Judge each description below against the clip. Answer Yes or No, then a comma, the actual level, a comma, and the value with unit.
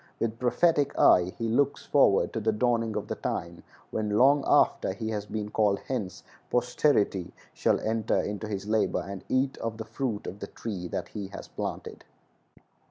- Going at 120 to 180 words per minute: Yes, average, 175 wpm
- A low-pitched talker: Yes, low, 110 Hz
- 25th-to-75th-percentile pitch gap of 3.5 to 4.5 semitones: No, average, 3.0 semitones